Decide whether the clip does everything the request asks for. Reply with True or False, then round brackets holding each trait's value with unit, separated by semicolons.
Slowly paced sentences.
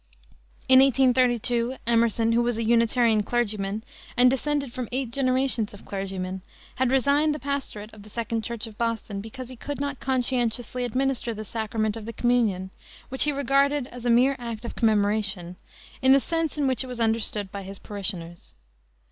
False (175 wpm)